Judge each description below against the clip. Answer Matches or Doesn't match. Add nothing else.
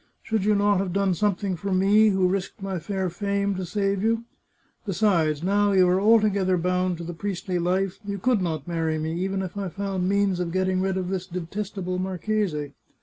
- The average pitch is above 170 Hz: Matches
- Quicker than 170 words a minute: Matches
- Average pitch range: Doesn't match